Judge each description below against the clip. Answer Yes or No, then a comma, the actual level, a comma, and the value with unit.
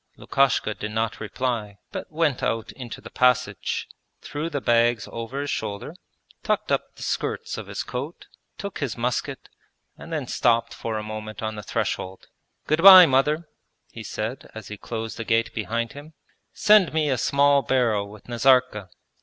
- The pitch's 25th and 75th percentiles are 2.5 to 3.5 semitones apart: No, average, 4.5 semitones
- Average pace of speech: Yes, average, 170 wpm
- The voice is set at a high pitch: No, low, 120 Hz